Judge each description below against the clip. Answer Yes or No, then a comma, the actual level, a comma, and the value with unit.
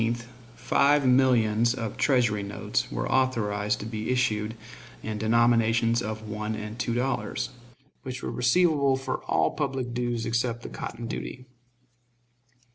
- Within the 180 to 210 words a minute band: No, average, 145 wpm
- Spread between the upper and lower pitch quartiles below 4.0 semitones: Yes, average, 2.8 semitones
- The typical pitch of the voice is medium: No, low, 120 Hz